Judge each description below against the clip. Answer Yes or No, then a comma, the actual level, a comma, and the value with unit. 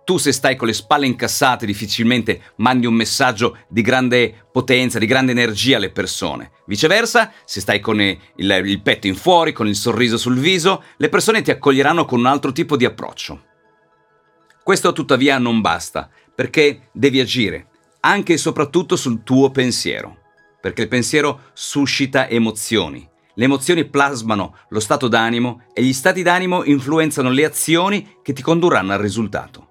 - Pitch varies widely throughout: No, average, 4.7 semitones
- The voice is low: Yes, low, 125 Hz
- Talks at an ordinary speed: Yes, average, 160 wpm